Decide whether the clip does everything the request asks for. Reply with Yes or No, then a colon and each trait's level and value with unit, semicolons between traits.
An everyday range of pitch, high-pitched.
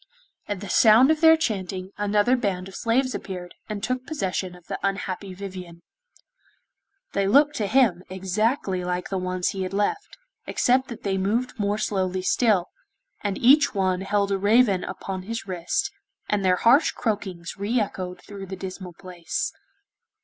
Yes: average, 3.5 semitones; high, 195 Hz